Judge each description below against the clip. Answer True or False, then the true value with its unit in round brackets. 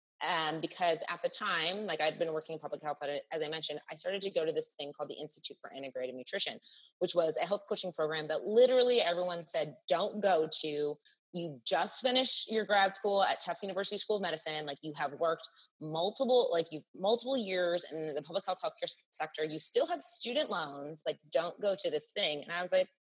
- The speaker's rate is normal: False (220 wpm)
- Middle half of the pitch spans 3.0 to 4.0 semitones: False (4.7 semitones)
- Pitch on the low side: False (170 Hz)